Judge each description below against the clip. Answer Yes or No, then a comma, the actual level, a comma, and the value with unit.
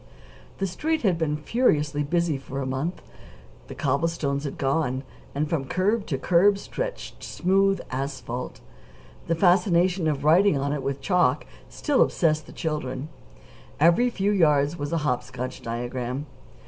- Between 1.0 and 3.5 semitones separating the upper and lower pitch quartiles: No, average, 4.8 semitones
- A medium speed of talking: Yes, average, 150 wpm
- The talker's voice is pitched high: No, medium, 155 Hz